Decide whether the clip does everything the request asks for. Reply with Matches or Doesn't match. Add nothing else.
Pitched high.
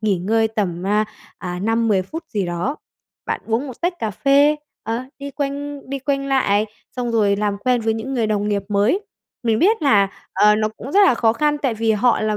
Matches